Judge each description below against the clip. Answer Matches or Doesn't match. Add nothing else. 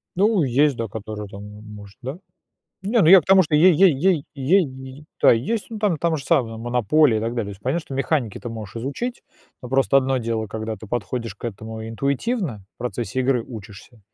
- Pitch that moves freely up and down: Matches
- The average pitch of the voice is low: Matches